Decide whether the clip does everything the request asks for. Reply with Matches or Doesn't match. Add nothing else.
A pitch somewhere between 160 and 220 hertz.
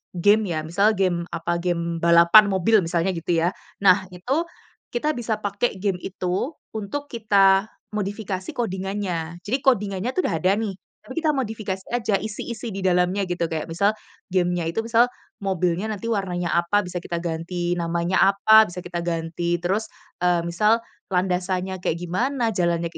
Matches